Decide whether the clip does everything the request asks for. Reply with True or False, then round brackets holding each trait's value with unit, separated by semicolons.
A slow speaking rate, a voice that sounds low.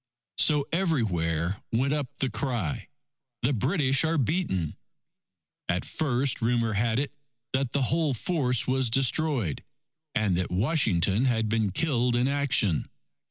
True (130 wpm; 125 Hz)